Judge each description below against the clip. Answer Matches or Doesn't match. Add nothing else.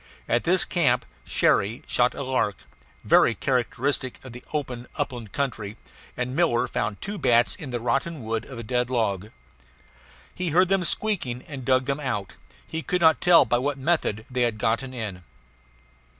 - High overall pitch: Doesn't match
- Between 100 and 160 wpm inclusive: Doesn't match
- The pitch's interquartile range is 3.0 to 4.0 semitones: Matches